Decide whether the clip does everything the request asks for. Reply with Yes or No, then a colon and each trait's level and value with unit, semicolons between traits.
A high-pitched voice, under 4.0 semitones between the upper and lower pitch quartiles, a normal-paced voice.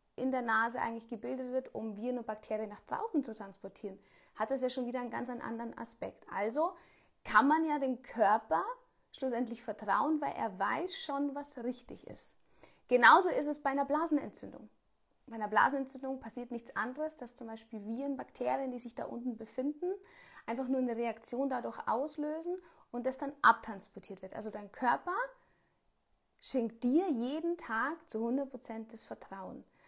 No: very high, 255 Hz; average, 4.4 semitones; average, 165 wpm